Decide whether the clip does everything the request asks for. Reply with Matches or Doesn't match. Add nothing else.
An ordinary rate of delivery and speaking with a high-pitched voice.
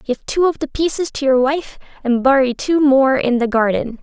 Doesn't match